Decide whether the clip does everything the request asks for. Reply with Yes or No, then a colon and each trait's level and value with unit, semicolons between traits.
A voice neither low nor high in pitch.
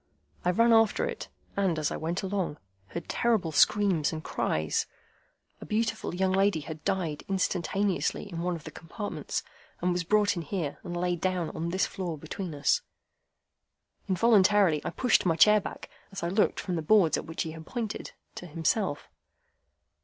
Yes: medium, 180 Hz